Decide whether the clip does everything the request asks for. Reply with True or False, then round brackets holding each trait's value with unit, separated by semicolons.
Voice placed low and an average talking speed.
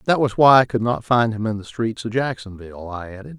False (110 Hz; 265 wpm)